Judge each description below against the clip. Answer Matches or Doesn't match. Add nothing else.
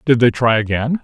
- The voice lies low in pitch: Matches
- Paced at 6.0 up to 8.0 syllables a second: Doesn't match